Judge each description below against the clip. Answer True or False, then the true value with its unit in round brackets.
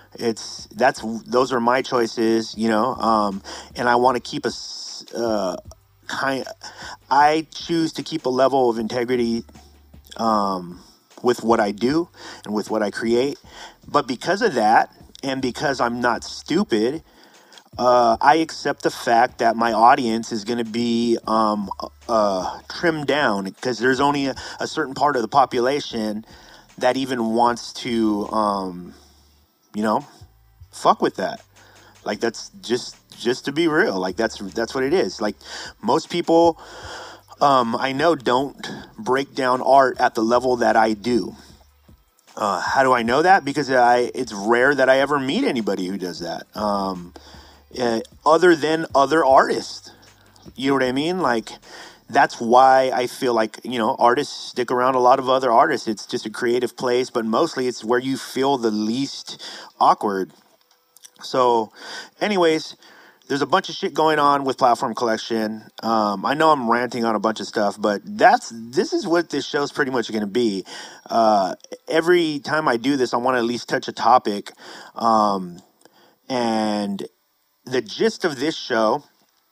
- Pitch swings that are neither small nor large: True (3.6 semitones)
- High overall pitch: False (120 Hz)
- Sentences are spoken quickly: False (170 wpm)